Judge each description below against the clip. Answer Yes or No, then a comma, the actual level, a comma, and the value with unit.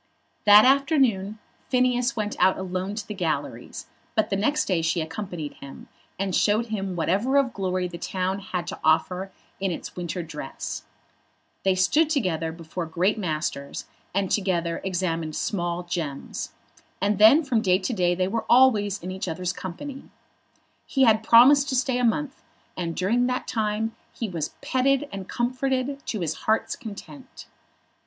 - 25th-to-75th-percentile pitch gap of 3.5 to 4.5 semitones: No, wide, 5.5 semitones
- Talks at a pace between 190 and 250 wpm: No, average, 160 wpm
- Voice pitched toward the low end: No, high, 195 Hz